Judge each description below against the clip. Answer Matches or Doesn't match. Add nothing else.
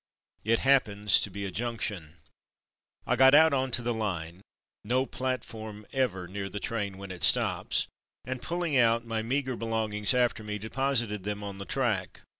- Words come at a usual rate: Matches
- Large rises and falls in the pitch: Doesn't match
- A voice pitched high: Doesn't match